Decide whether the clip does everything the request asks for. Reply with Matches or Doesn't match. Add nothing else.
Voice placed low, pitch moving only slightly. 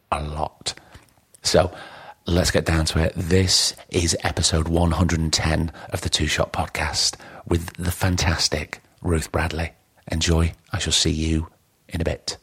Matches